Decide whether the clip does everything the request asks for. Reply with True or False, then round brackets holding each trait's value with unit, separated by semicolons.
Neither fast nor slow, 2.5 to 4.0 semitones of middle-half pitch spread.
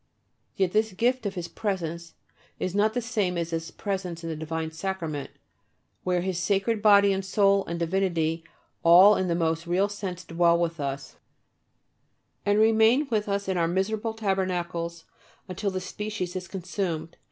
True (165 wpm; 3.2 semitones)